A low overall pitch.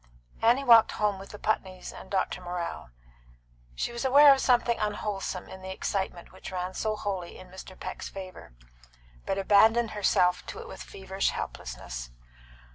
No: high, 195 Hz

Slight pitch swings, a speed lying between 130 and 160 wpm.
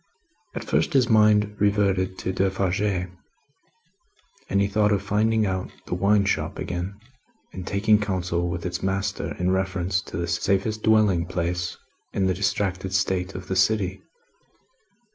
Yes: narrow, 2.3 semitones; average, 145 wpm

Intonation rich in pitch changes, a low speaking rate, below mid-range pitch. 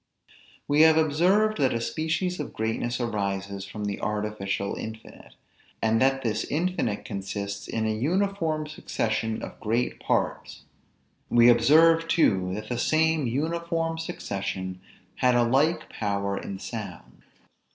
Yes: wide, 7.2 semitones; slow, 130 wpm; low, 120 Hz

